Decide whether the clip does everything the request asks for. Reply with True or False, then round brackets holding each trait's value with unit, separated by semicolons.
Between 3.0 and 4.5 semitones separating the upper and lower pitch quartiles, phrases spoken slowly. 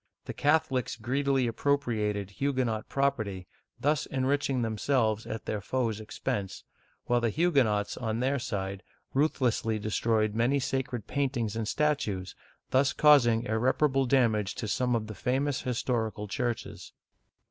True (4.0 semitones; 125 wpm)